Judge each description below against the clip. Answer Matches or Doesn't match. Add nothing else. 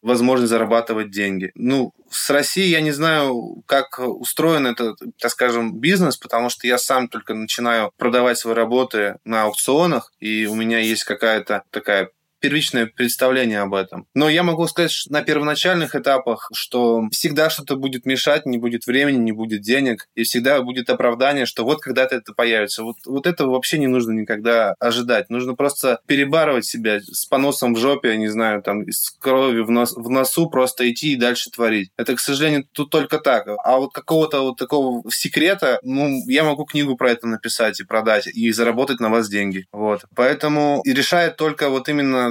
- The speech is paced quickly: Matches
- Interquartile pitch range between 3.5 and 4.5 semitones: Matches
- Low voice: Matches